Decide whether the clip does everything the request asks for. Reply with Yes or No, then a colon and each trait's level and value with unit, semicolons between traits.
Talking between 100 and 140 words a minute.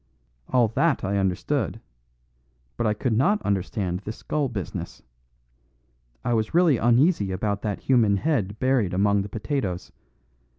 Yes: slow, 135 wpm